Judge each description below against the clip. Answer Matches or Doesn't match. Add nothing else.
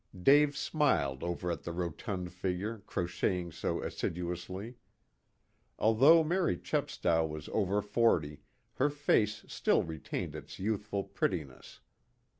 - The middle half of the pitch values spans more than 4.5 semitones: Matches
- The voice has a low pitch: Matches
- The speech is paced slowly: Matches